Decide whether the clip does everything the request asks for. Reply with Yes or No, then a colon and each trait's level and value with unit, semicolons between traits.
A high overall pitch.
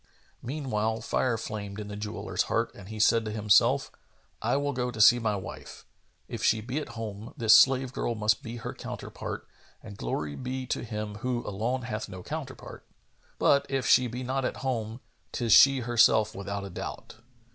No: low, 115 Hz